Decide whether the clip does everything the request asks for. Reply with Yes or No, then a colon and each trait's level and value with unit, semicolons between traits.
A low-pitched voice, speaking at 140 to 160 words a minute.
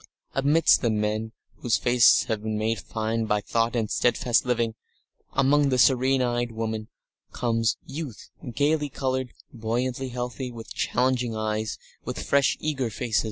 Yes: low, 120 Hz; average, 150 wpm